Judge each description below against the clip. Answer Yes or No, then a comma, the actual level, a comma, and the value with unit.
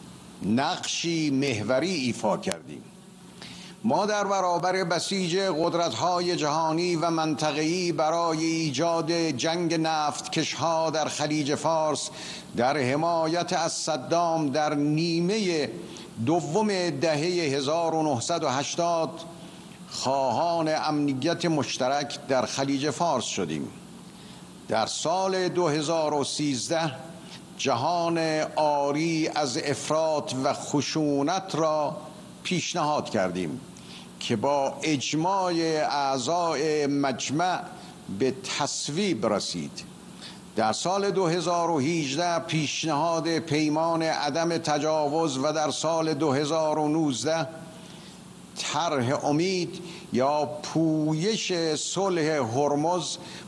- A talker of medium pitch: Yes, medium, 160 Hz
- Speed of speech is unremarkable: No, slow, 80 wpm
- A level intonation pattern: Yes, narrow, 2.2 semitones